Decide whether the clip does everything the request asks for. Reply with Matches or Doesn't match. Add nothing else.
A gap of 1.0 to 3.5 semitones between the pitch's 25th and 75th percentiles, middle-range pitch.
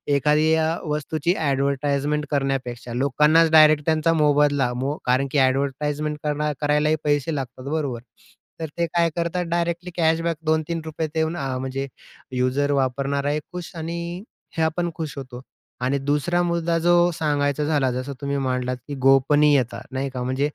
Matches